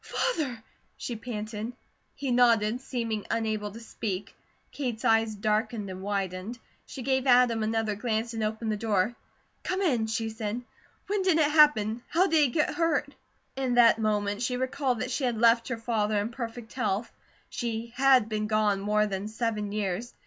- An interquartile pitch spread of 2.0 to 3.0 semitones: Yes, average, 2.7 semitones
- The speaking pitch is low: No, high, 225 Hz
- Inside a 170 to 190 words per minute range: Yes, average, 175 wpm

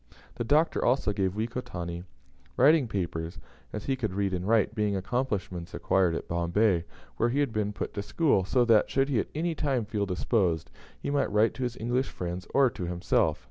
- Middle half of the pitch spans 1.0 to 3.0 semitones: No, wide, 5.5 semitones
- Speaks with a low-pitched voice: Yes, low, 105 Hz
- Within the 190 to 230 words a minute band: Yes, average, 195 wpm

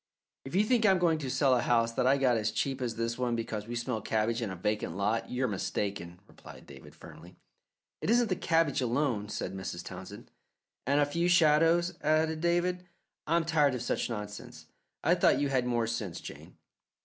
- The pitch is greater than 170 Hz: No, low, 125 Hz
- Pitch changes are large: Yes, wide, 6.6 semitones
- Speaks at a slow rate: No, average, 200 wpm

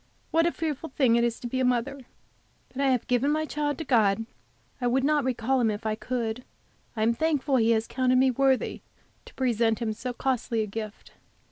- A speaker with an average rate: No, fast, 215 wpm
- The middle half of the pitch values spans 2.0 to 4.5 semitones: Yes, average, 3.0 semitones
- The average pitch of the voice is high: Yes, very high, 250 Hz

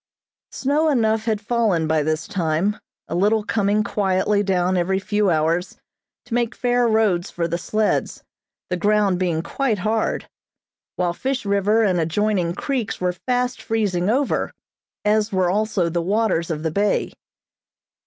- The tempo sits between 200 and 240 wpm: No, average, 150 wpm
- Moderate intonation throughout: Yes, average, 3.9 semitones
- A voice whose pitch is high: Yes, high, 205 Hz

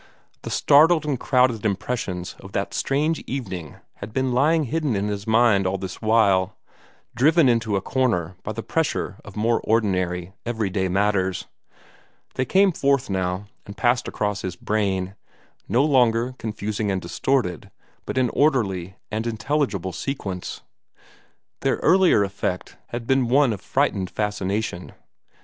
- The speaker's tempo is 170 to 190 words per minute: No, average, 140 wpm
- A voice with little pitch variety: No, average, 5.2 semitones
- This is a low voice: Yes, low, 110 Hz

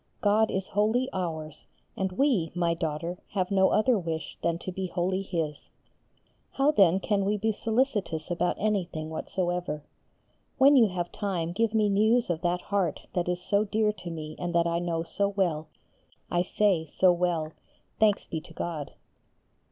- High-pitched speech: No, medium, 180 Hz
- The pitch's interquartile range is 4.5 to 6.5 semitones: No, average, 3.6 semitones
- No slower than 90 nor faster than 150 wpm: No, average, 170 wpm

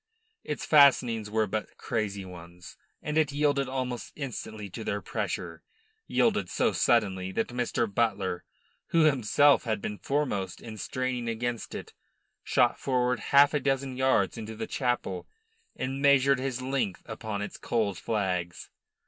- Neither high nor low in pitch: No, low, 120 Hz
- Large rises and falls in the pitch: No, average, 4.5 semitones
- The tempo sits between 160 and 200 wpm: No, average, 145 wpm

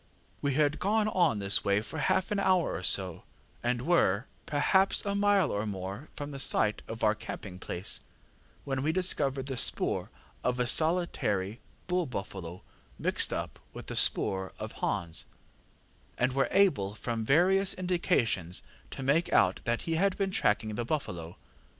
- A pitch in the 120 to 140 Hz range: Yes, low, 135 Hz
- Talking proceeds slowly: No, average, 165 wpm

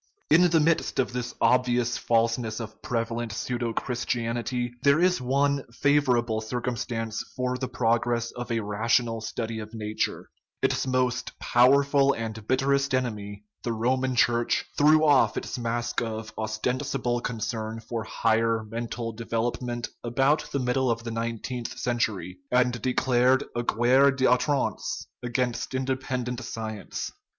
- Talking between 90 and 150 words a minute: Yes, average, 140 wpm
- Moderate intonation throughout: No, narrow, 2.1 semitones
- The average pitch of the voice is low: Yes, low, 120 Hz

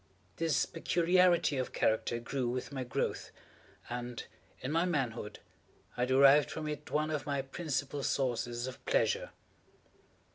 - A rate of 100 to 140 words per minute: Yes, slow, 135 wpm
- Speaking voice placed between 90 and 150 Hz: Yes, medium, 140 Hz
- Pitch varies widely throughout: No, average, 4.3 semitones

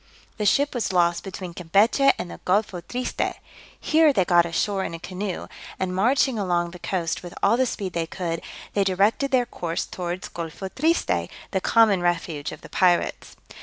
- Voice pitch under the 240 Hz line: Yes, medium, 185 Hz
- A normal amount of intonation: Yes, average, 4.1 semitones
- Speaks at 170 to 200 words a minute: Yes, average, 180 wpm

